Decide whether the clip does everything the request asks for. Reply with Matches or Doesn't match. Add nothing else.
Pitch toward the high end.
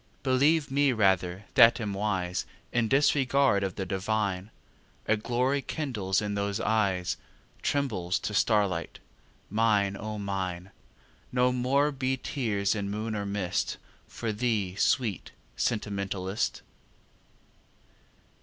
Doesn't match